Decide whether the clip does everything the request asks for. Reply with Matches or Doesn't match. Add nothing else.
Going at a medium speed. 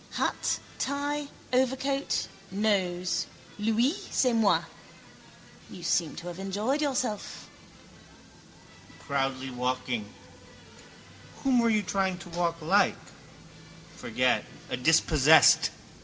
Doesn't match